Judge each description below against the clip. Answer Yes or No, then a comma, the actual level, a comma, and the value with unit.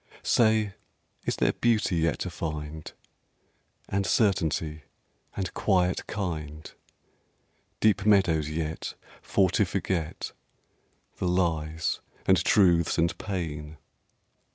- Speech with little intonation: No, average, 3.8 semitones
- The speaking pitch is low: Yes, very low, 85 Hz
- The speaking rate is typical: No, slow, 100 wpm